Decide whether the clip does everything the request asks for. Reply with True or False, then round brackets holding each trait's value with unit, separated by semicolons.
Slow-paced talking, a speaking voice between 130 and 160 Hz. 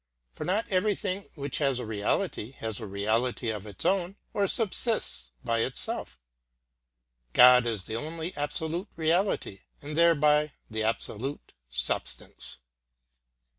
True (125 wpm; 140 Hz)